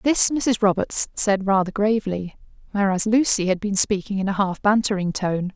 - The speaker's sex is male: No, female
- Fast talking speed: No, average, 175 wpm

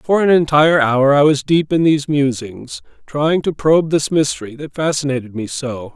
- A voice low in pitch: No, medium, 145 Hz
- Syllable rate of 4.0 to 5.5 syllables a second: Yes, 5.1 syllables/s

